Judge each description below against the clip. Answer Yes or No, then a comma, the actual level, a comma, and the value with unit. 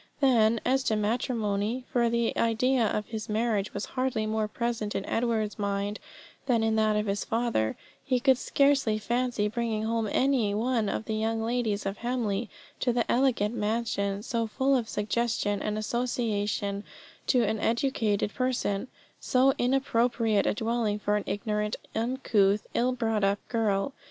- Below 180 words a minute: Yes, average, 155 wpm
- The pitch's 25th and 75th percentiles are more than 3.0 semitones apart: No, narrow, 2.6 semitones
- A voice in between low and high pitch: No, high, 225 Hz